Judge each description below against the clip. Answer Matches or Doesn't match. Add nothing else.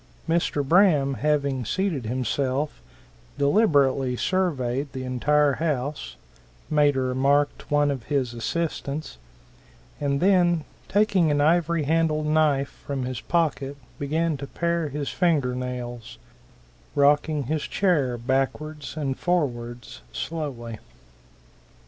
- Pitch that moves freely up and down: Doesn't match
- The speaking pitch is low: Doesn't match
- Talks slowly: Matches